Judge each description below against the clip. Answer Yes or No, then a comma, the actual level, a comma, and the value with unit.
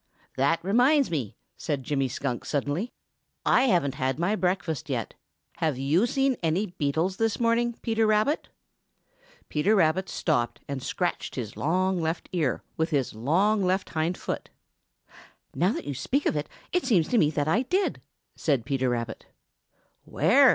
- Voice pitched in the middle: Yes, medium, 165 Hz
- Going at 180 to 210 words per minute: No, average, 155 wpm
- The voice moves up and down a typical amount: No, wide, 7.1 semitones